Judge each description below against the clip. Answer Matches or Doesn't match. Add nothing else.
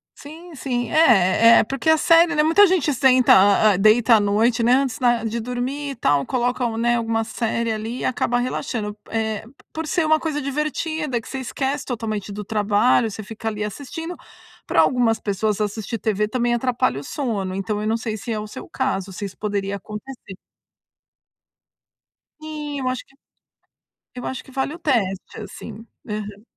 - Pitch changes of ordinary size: Matches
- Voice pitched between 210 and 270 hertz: Matches